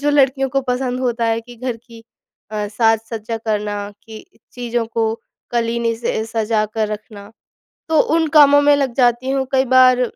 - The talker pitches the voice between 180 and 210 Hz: No, high, 235 Hz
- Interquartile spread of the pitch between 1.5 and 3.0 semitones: Yes, average, 2.7 semitones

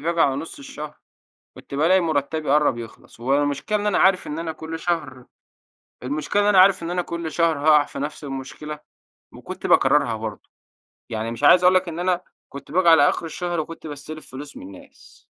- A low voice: No, medium, 155 Hz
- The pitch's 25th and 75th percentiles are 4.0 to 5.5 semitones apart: No, average, 3.4 semitones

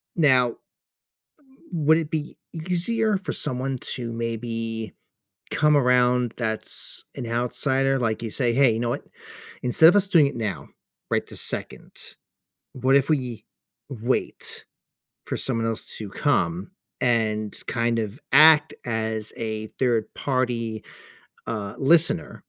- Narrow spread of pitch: No, average, 4.1 semitones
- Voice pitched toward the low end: Yes, low, 125 Hz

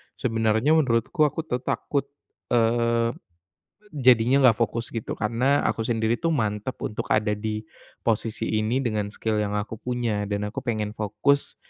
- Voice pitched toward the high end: No, low, 115 Hz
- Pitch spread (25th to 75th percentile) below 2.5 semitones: No, average, 2.8 semitones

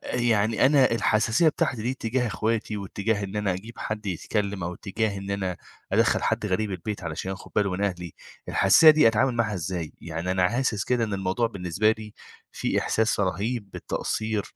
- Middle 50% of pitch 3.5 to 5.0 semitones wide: No, average, 3.0 semitones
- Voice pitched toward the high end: No, low, 105 Hz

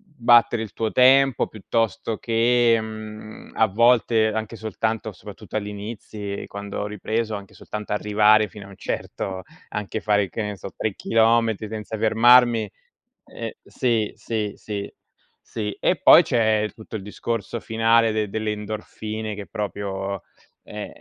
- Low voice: Yes, low, 110 Hz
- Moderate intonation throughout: No, narrow, 1.6 semitones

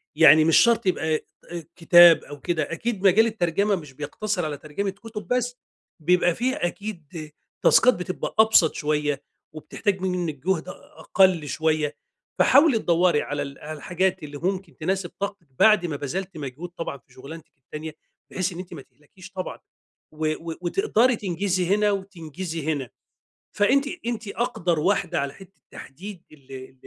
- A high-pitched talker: No, medium, 175 Hz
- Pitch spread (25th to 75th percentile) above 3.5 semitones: Yes, average, 4.4 semitones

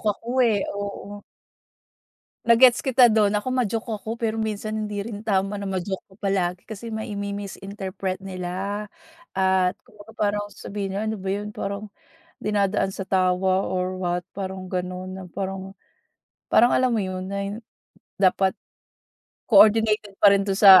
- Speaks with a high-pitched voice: Yes, high, 200 Hz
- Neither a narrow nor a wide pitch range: No, narrow, 2.0 semitones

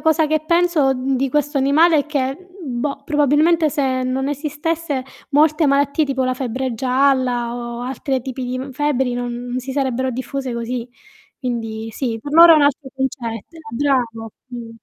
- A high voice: Yes, very high, 265 Hz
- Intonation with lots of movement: No, average, 2.9 semitones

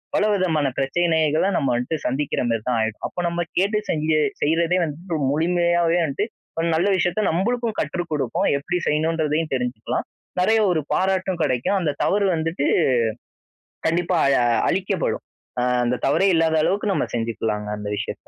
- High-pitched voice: No, medium, 165 Hz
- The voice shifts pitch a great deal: No, average, 3.8 semitones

